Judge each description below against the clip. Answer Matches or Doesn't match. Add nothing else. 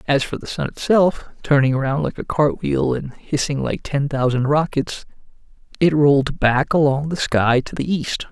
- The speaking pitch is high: Doesn't match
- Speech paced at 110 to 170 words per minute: Doesn't match